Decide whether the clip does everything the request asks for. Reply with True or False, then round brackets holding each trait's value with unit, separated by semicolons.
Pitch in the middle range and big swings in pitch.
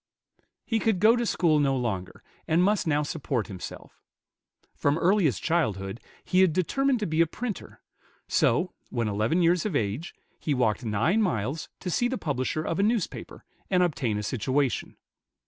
True (155 Hz; 7.4 semitones)